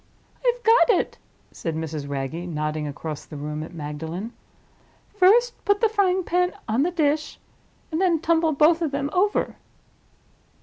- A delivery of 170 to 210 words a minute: No, average, 150 wpm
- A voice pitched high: Yes, very high, 290 Hz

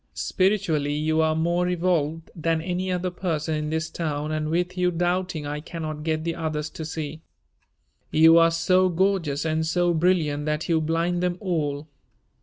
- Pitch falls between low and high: Yes, medium, 165 Hz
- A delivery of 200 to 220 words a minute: No, average, 170 wpm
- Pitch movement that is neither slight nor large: No, narrow, 2.3 semitones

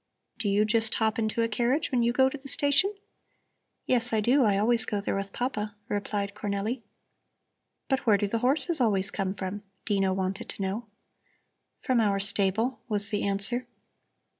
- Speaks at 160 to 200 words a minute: Yes, average, 175 wpm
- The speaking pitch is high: Yes, high, 215 Hz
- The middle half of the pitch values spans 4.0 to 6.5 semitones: No, average, 3.4 semitones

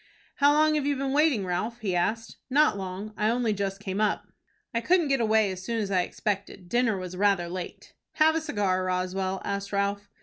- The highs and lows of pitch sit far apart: No, average, 4.5 semitones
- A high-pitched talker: Yes, high, 205 Hz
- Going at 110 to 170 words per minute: No, fast, 205 wpm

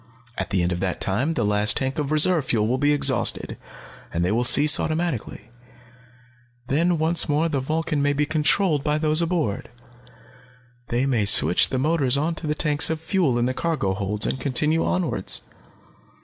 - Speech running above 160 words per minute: Yes, average, 175 wpm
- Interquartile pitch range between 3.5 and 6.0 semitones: Yes, average, 4.8 semitones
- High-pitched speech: No, medium, 145 Hz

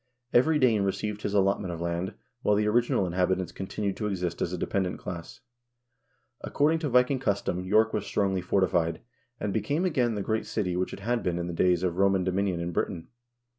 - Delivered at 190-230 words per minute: Yes, average, 200 wpm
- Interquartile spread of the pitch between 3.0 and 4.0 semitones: Yes, average, 3.4 semitones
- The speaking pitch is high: No, very low, 95 Hz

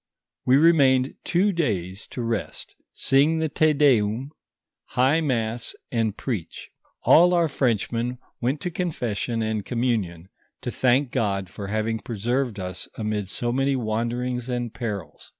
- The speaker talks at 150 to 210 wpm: No, slow, 135 wpm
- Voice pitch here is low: Yes, low, 120 Hz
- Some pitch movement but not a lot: Yes, average, 4.0 semitones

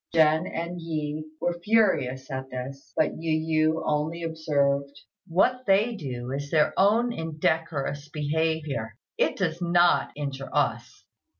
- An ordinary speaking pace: No, slow, 130 wpm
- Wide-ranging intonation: No, average, 3.1 semitones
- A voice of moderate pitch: Yes, medium, 155 Hz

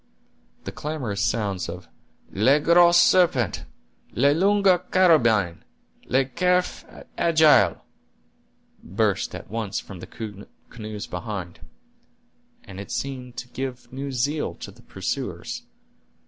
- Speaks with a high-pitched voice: No, low, 125 Hz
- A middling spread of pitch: No, wide, 7.3 semitones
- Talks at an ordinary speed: No, slow, 105 wpm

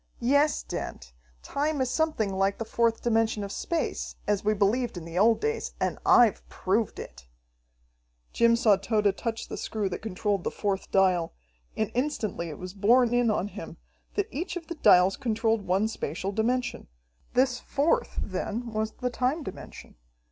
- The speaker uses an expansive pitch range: No, average, 4.1 semitones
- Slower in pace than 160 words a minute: No, average, 170 wpm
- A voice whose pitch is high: Yes, high, 220 Hz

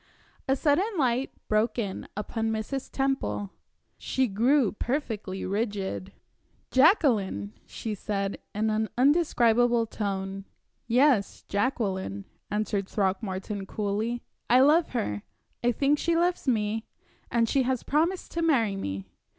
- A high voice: Yes, high, 225 Hz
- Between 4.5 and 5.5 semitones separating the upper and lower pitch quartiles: Yes, average, 5.1 semitones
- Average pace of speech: No, slow, 120 wpm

